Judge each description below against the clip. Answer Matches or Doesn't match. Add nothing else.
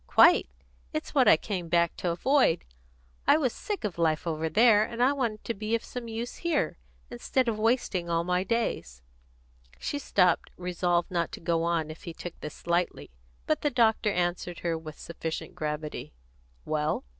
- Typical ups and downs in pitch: Doesn't match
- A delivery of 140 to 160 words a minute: Doesn't match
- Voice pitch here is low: Doesn't match